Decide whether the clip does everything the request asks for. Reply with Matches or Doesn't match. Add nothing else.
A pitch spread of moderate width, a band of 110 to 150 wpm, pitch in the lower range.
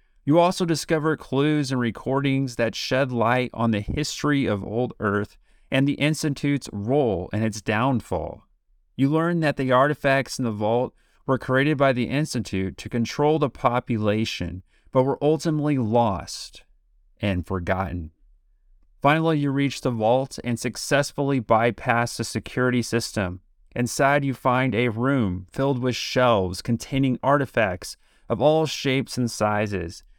Matches